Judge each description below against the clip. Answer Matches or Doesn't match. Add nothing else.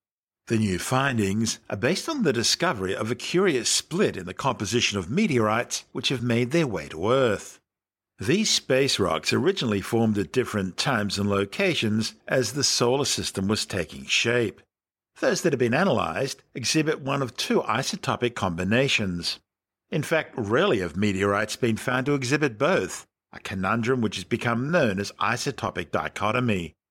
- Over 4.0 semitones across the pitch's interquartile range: Matches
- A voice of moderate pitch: Doesn't match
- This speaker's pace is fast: Doesn't match